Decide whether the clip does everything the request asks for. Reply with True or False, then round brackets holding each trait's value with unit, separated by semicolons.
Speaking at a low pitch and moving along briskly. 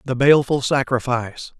False (130 Hz; 115 wpm)